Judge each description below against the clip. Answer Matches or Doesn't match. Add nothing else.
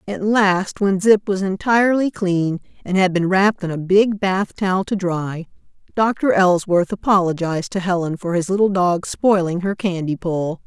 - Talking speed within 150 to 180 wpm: Matches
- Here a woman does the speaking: Matches